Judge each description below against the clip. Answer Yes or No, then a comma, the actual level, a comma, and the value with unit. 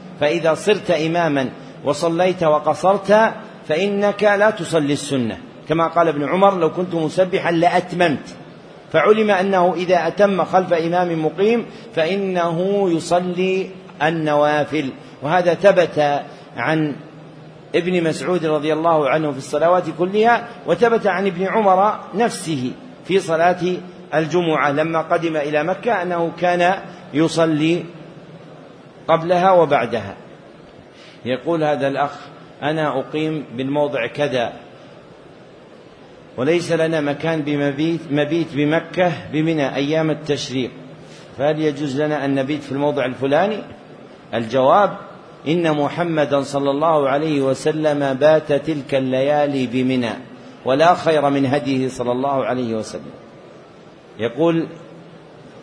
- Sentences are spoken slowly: No, average, 105 wpm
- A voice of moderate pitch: Yes, medium, 160 Hz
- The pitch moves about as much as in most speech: Yes, average, 3.7 semitones